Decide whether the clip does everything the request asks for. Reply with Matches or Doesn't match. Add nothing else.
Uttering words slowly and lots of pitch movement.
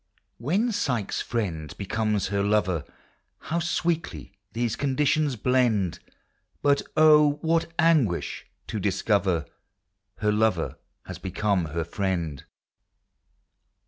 Matches